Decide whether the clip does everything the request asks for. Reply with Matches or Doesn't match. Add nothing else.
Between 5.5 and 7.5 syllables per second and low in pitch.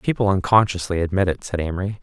Matches